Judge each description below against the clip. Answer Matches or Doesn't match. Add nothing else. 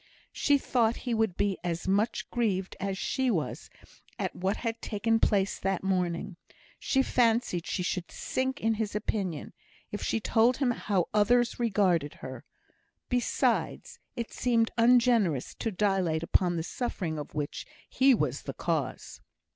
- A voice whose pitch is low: Doesn't match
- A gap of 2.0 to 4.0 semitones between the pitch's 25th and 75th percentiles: Doesn't match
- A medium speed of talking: Matches